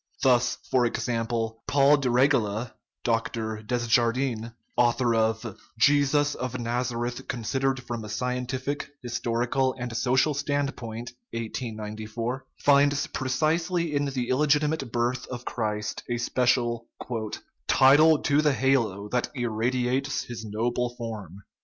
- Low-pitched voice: Yes, low, 125 Hz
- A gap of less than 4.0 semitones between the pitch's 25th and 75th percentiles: Yes, average, 2.7 semitones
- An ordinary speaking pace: No, slow, 120 wpm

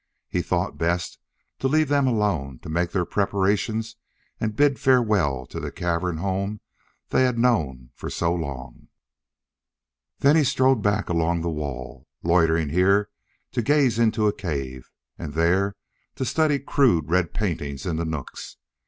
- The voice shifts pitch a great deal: Yes, wide, 6.1 semitones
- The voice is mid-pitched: No, very low, 95 Hz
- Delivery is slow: No, average, 155 wpm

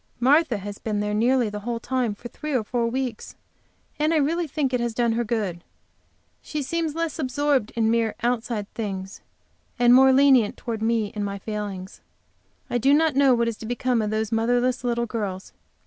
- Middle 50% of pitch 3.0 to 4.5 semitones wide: Yes, average, 3.5 semitones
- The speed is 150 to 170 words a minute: No, average, 195 wpm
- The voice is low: No, high, 235 Hz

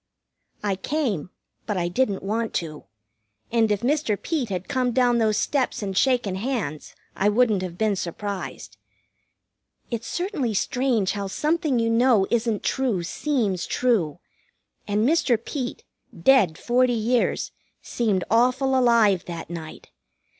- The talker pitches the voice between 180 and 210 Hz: No, high, 230 Hz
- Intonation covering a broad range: No, average, 4.5 semitones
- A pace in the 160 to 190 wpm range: No, slow, 135 wpm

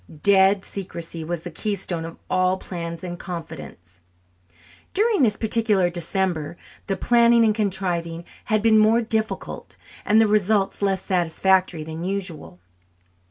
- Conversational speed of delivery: No, slow, 130 wpm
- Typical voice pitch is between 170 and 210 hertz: Yes, high, 190 Hz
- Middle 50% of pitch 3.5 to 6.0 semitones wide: Yes, average, 4.0 semitones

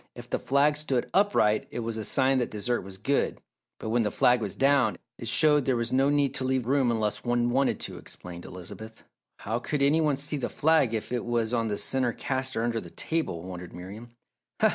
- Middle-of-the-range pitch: No, low, 120 Hz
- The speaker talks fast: Yes, fast, 215 wpm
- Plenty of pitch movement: No, average, 3.8 semitones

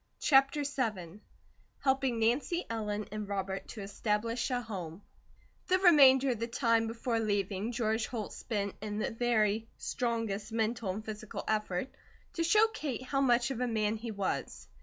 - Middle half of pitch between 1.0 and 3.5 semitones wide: Yes, average, 3.2 semitones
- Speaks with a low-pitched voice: No, high, 225 Hz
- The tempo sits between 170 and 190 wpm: No, average, 160 wpm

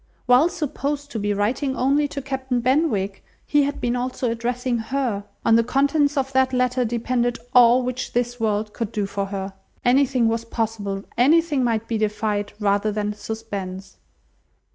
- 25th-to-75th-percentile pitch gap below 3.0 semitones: No, average, 3.7 semitones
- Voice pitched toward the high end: Yes, high, 240 Hz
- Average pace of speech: Yes, average, 165 wpm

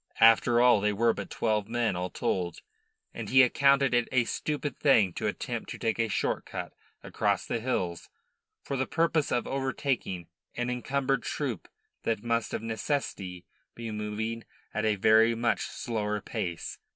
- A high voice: No, low, 115 Hz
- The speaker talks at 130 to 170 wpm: Yes, average, 165 wpm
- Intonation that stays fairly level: No, average, 3.4 semitones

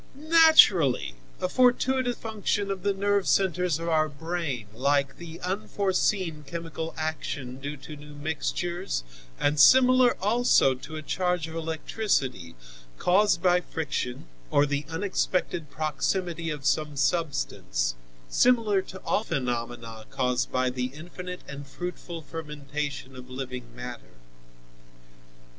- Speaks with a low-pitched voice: No, medium, 160 Hz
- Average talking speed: No, slow, 120 wpm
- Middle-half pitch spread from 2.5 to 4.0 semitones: No, average, 5.3 semitones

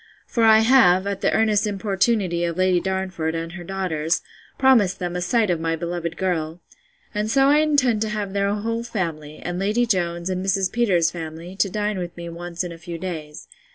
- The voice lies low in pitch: No, medium, 185 Hz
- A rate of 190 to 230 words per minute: Yes, average, 200 wpm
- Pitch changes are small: No, average, 3.7 semitones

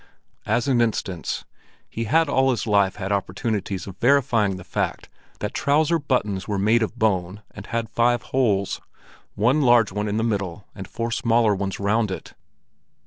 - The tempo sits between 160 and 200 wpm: Yes, average, 170 wpm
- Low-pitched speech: Yes, low, 110 Hz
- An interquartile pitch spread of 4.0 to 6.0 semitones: No, average, 3.4 semitones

